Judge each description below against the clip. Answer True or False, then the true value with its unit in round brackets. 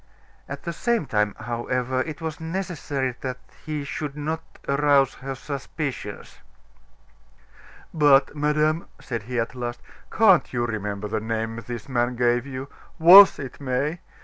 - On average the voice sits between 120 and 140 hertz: True (135 Hz)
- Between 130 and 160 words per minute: True (140 wpm)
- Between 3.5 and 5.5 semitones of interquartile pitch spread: True (4.0 semitones)